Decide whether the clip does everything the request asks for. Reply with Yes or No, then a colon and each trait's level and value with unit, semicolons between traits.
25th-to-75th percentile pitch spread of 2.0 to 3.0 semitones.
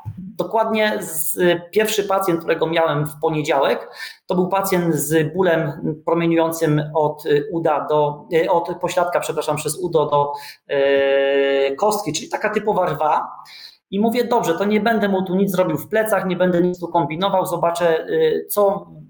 No: average, 4.3 semitones